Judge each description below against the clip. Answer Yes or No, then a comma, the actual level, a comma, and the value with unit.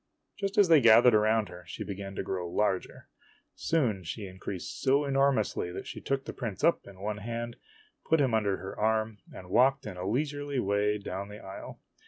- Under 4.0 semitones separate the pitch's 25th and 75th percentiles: No, wide, 5.6 semitones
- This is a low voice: Yes, low, 110 Hz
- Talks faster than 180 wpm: Yes, average, 195 wpm